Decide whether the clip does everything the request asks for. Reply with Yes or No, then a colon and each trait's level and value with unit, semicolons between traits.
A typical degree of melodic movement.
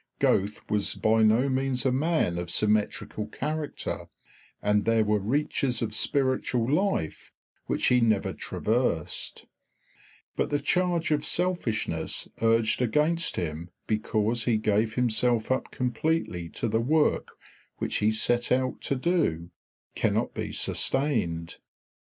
Yes: average, 4.6 semitones